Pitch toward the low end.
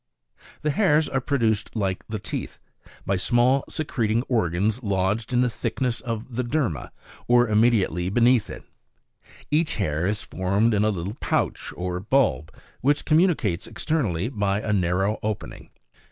Yes: low, 110 Hz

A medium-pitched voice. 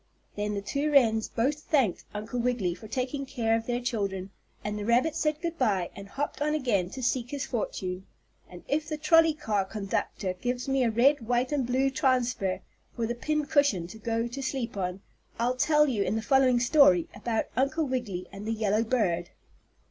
No: high, 240 Hz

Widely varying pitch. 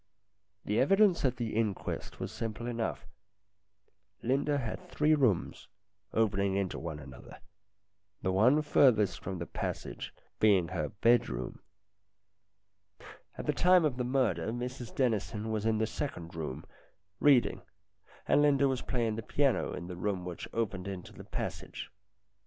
Yes: wide, 5.7 semitones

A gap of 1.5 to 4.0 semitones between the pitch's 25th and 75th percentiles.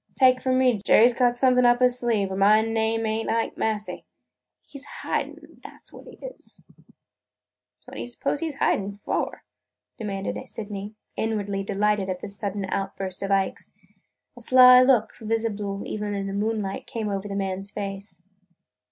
Yes: average, 3.4 semitones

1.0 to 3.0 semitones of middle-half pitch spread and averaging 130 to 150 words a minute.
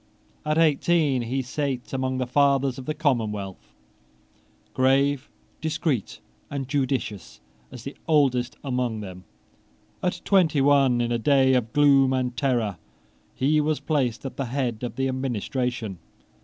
Yes: average, 2.7 semitones; average, 140 wpm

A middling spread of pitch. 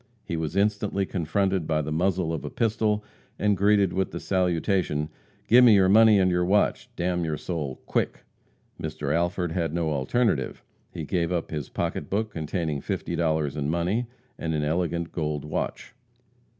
Yes: average, 3.9 semitones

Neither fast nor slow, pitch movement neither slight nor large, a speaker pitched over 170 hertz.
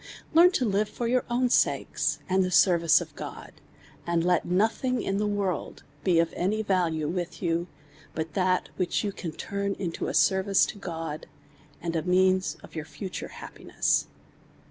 Yes: average, 170 wpm; average, 3.1 semitones; medium, 185 Hz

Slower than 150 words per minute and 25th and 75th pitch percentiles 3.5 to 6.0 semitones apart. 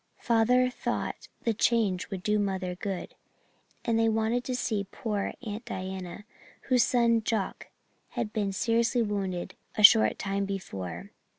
No: average, 140 wpm; average, 3.0 semitones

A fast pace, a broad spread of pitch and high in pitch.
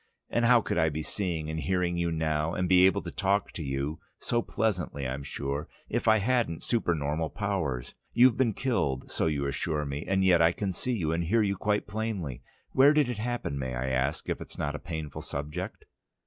No: fast, 210 wpm; wide, 6.0 semitones; very low, 85 Hz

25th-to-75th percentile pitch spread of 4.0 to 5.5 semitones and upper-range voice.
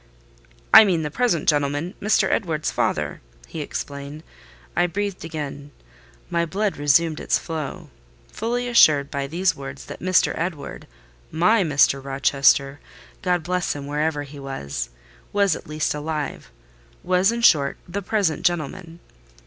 No: average, 4.4 semitones; medium, 155 Hz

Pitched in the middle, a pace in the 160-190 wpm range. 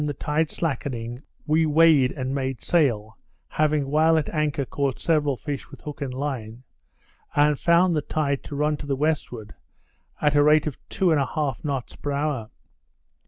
Yes: medium, 145 Hz; average, 175 wpm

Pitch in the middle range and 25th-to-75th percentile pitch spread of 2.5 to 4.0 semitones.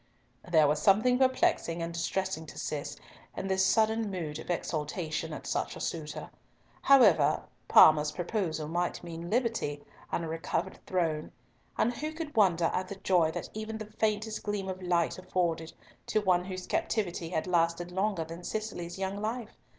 No: medium, 180 Hz; average, 4.5 semitones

